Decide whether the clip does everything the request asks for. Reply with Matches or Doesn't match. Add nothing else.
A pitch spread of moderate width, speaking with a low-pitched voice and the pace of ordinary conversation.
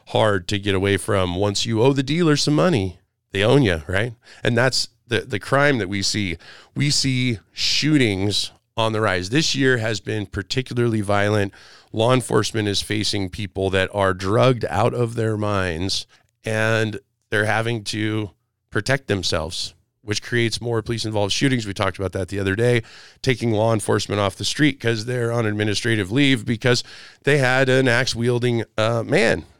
Matches